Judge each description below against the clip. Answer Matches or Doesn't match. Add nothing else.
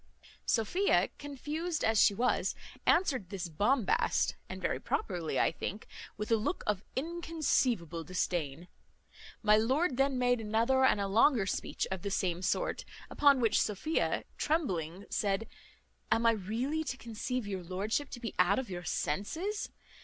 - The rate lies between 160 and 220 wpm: Doesn't match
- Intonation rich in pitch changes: Matches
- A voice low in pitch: Doesn't match